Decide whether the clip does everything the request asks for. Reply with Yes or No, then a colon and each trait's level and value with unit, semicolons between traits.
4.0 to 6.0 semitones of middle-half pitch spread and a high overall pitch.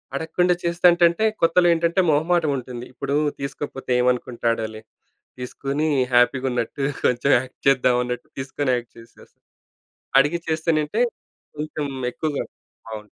No: average, 4.7 semitones; medium, 140 Hz